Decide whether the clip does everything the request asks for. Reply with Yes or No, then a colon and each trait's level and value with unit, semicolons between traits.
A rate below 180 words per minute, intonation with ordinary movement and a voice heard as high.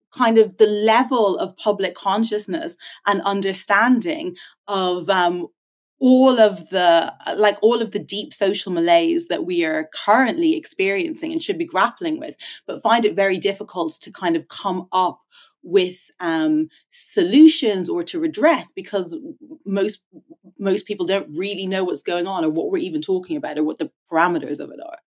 No: average, 165 wpm; wide, 8.8 semitones; high, 220 Hz